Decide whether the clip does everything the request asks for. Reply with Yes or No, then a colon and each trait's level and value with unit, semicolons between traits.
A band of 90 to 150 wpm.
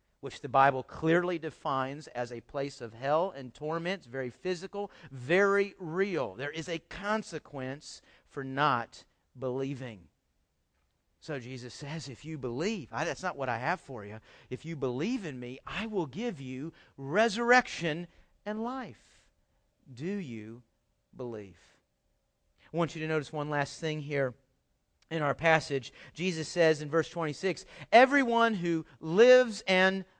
Yes: average, 145 wpm